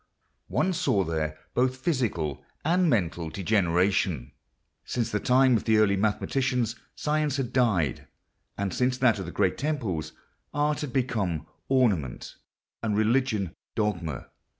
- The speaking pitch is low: Yes, low, 110 Hz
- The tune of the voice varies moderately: No, wide, 6.5 semitones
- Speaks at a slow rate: Yes, slow, 130 wpm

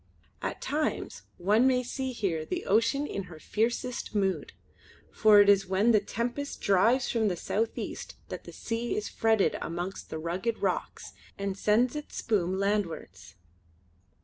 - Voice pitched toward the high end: Yes, high, 210 Hz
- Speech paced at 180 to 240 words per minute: No, average, 155 wpm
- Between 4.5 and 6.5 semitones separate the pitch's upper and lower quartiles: No, average, 3.8 semitones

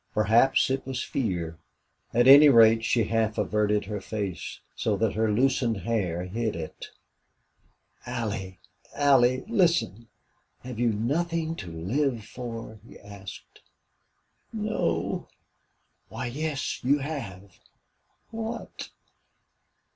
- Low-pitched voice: Yes, low, 115 Hz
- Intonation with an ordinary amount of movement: Yes, average, 4.7 semitones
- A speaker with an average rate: No, slow, 110 wpm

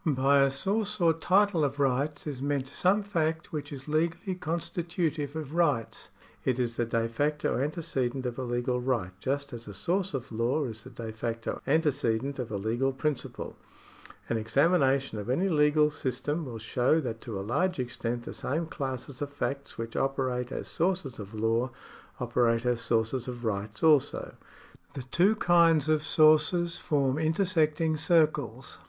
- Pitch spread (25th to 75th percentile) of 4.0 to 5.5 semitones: Yes, average, 4.6 semitones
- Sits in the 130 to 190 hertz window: Yes, medium, 140 Hz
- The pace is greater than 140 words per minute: Yes, average, 165 wpm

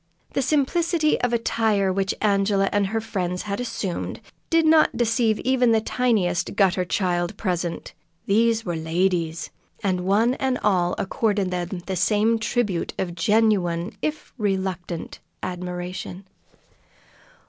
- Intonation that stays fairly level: No, average, 4.1 semitones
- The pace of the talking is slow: Yes, slow, 125 wpm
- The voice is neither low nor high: No, high, 200 Hz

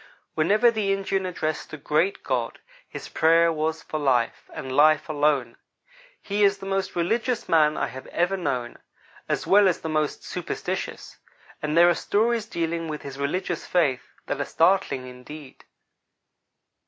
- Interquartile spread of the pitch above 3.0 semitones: Yes, average, 5.0 semitones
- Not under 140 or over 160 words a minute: Yes, average, 155 wpm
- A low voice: No, medium, 160 Hz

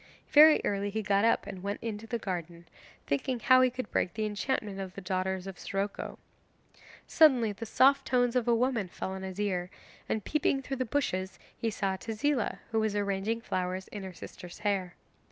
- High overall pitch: Yes, high, 205 Hz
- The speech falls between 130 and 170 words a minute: No, average, 190 wpm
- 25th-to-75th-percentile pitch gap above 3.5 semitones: Yes, average, 4.0 semitones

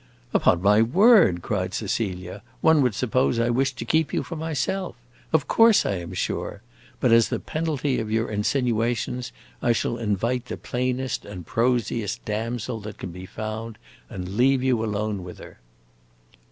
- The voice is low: Yes, low, 115 Hz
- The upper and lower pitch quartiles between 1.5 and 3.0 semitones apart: No, average, 3.8 semitones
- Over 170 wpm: No, average, 165 wpm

